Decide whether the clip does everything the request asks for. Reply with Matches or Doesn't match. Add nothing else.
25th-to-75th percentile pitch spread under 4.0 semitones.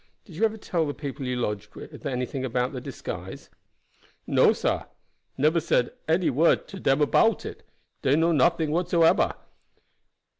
Doesn't match